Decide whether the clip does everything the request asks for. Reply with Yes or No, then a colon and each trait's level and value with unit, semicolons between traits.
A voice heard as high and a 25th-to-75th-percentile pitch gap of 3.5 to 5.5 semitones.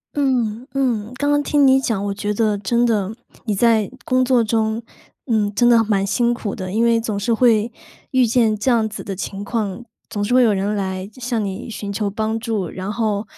No: high, 220 Hz; average, 2.8 semitones